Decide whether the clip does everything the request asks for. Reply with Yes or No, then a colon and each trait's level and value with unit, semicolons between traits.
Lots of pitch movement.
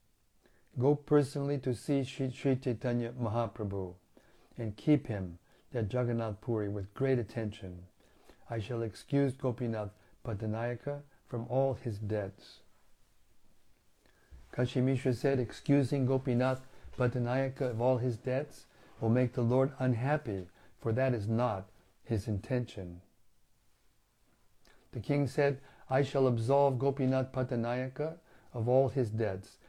No: average, 3.7 semitones